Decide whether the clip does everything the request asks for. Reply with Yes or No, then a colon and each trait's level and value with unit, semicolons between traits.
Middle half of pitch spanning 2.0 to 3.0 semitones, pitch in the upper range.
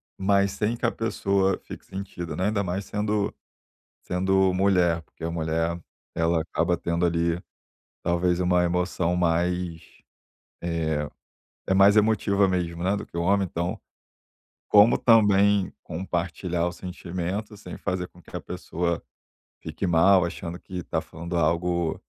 No: narrow, 2.4 semitones; very low, 90 Hz